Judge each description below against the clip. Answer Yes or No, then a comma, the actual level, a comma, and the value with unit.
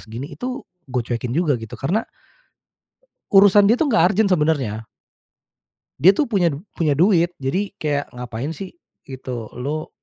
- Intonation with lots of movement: Yes, wide, 7.5 semitones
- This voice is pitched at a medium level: Yes, medium, 155 Hz